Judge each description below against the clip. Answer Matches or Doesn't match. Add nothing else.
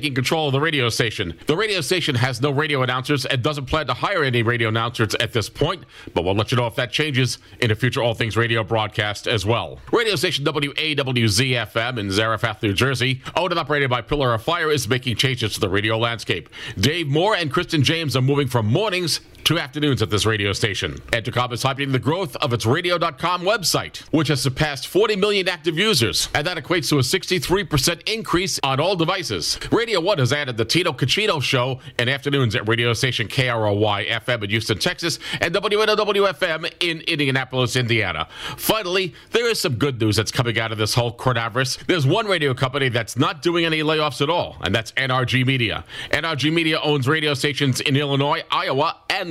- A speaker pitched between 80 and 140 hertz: Matches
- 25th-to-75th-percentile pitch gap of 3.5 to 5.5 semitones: Matches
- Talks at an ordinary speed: Matches